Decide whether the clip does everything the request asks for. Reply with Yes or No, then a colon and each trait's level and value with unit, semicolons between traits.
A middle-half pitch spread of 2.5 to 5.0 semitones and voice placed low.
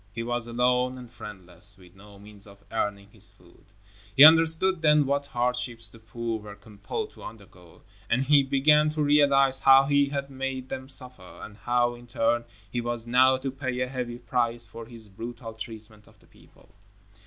Yes: average, 3.5 semitones; low, 120 Hz